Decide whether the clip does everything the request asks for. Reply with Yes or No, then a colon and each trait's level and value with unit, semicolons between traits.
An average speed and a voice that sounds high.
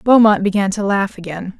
Yes: average, 190 wpm; high, 200 Hz